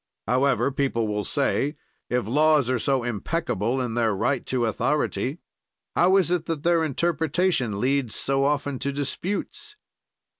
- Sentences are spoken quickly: No, average, 145 wpm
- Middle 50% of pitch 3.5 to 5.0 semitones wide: Yes, average, 4.3 semitones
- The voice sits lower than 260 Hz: Yes, medium, 140 Hz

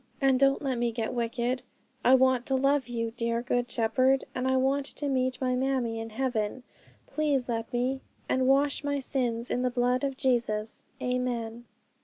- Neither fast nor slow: Yes, average, 180 wpm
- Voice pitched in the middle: No, very high, 255 Hz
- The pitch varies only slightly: Yes, narrow, 2.1 semitones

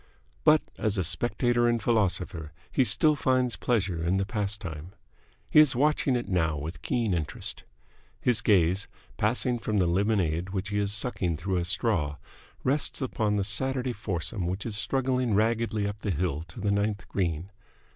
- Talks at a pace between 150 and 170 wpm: Yes, average, 165 wpm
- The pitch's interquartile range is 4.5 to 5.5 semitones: Yes, average, 4.9 semitones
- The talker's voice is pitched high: No, low, 100 Hz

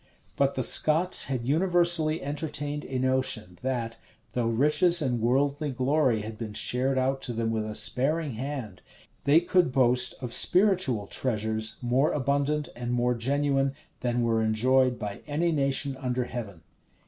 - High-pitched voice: No, low, 130 Hz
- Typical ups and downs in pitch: Yes, average, 3.7 semitones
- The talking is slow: No, average, 155 wpm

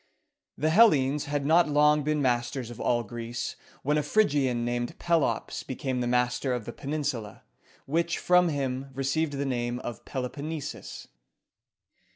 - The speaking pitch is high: No, medium, 140 Hz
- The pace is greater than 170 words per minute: No, average, 160 wpm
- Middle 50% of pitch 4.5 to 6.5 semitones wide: No, average, 3.5 semitones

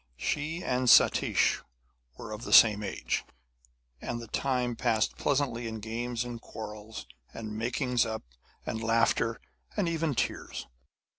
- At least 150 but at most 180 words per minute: No, slow, 135 wpm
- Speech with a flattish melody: Yes, narrow, 2.2 semitones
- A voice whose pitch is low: Yes, low, 115 Hz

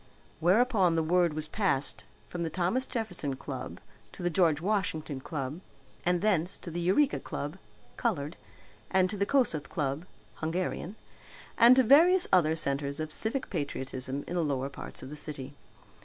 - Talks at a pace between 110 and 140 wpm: No, average, 160 wpm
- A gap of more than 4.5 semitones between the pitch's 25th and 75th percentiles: Yes, average, 5.2 semitones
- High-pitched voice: No, medium, 170 Hz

